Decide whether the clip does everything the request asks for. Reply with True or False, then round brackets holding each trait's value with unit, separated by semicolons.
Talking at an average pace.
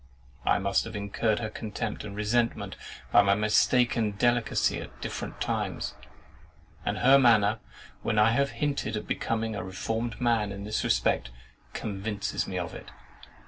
True (150 wpm)